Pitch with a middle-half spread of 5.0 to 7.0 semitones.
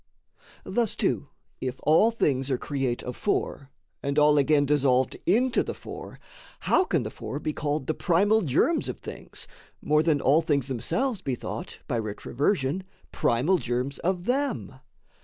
Yes: wide, 5.6 semitones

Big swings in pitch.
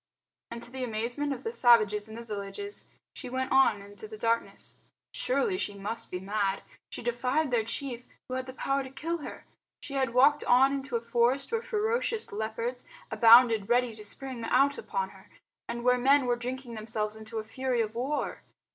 No: average, 3.5 semitones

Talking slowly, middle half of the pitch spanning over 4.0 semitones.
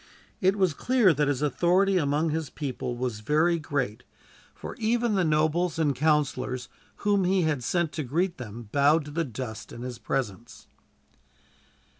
No: average, 160 wpm; wide, 5.4 semitones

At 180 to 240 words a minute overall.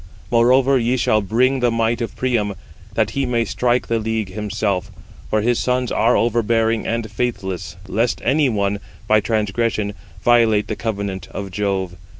No: average, 160 wpm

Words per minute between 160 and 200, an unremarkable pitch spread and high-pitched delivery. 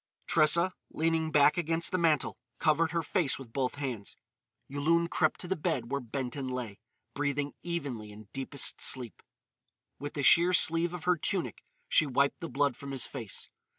No: average, 170 wpm; average, 4.0 semitones; medium, 145 Hz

